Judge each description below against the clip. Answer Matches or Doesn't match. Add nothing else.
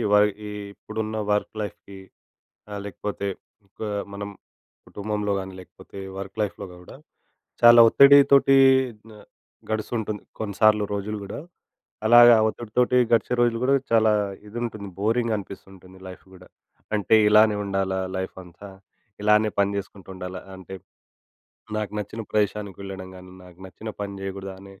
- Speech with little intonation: Matches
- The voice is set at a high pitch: Doesn't match